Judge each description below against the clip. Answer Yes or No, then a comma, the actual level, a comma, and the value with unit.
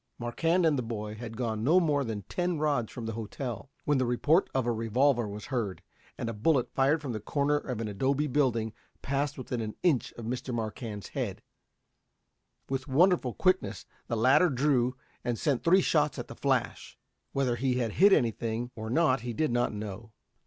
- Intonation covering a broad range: No, average, 4.3 semitones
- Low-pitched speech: Yes, low, 125 Hz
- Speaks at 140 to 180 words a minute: No, average, 195 wpm